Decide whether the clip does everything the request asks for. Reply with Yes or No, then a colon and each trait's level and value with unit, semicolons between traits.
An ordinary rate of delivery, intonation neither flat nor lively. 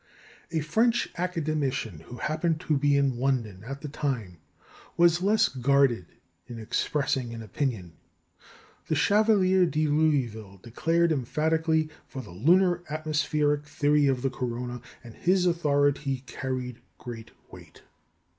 No: slow, 130 wpm; average, 4.5 semitones